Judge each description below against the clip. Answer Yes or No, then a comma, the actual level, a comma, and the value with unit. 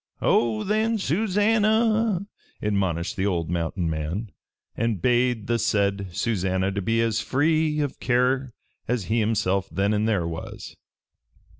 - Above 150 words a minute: No, slow, 135 wpm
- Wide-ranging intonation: Yes, wide, 6.8 semitones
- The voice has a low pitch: Yes, low, 115 Hz